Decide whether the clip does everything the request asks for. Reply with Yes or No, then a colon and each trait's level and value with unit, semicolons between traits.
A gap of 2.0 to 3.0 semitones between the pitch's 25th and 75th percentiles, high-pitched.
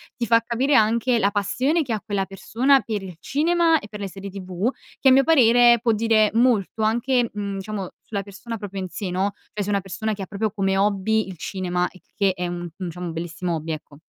No: average, 3.6 semitones; high, 205 Hz